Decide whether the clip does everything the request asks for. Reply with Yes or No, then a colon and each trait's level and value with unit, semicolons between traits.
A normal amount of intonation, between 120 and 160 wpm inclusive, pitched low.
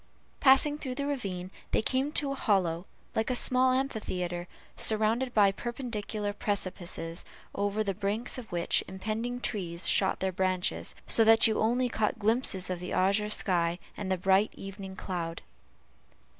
No: average, 4.3 semitones; average, 155 wpm; high, 205 Hz